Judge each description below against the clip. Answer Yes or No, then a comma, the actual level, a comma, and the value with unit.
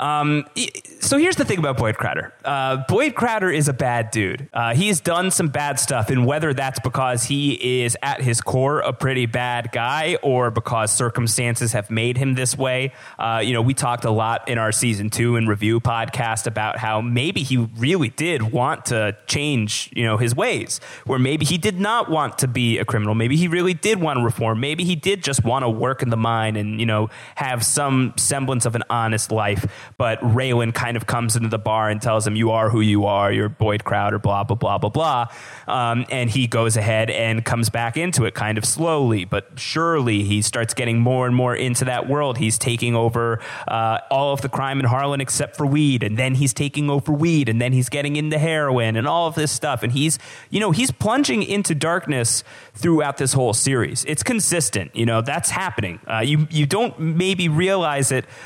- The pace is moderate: No, fast, 215 wpm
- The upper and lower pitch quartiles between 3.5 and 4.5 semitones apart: Yes, average, 4.2 semitones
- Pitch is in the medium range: No, low, 125 Hz